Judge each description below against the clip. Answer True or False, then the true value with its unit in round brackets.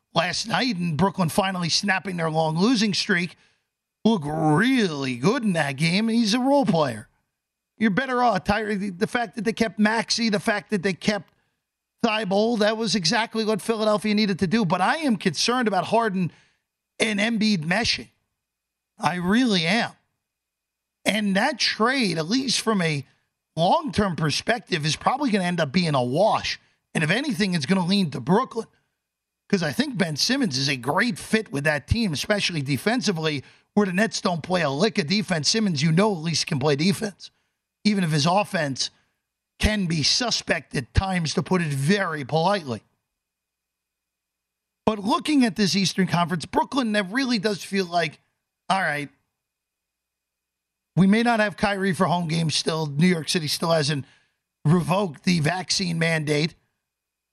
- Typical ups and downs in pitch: False (5.9 semitones)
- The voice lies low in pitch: False (190 Hz)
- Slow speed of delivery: False (170 wpm)